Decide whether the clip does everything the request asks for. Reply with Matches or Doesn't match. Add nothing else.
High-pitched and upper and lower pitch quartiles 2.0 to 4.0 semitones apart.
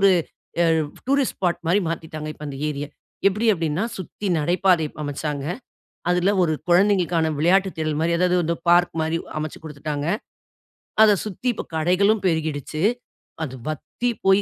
Doesn't match